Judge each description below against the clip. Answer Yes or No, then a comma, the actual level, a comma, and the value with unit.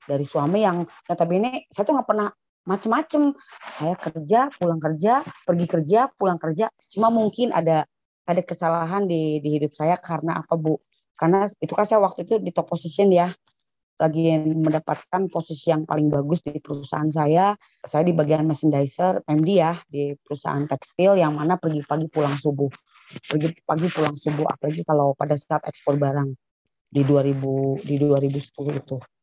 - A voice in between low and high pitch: Yes, medium, 160 Hz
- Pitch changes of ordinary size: Yes, average, 3.6 semitones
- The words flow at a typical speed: No, fast, 165 wpm